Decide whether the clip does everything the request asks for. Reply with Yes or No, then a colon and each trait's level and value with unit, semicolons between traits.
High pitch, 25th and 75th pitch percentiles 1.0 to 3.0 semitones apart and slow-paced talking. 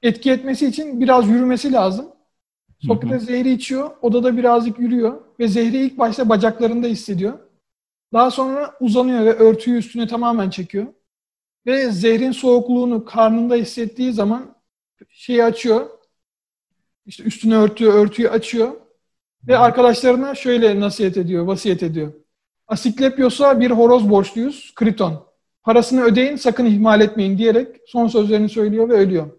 No: high, 235 Hz; narrow, 2.4 semitones; average, 125 wpm